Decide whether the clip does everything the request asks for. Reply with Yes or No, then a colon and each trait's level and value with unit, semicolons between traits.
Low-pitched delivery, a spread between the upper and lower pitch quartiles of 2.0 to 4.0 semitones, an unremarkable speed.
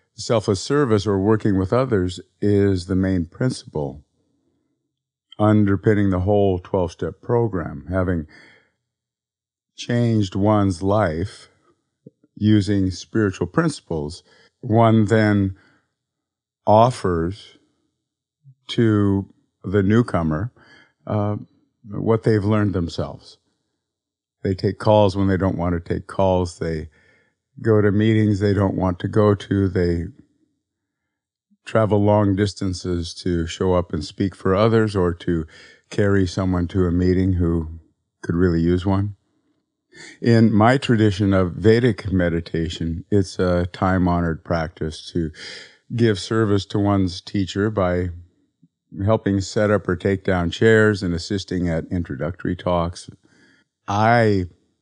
No: low, 100 Hz; average, 3.2 semitones; slow, 115 wpm